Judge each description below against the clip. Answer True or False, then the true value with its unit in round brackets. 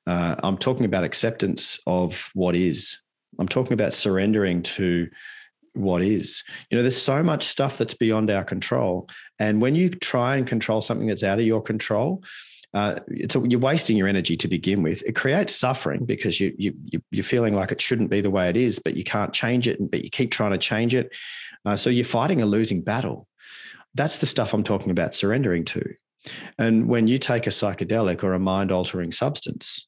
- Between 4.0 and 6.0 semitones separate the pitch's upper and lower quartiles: True (4.4 semitones)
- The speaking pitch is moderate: False (110 Hz)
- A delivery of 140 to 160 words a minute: False (200 wpm)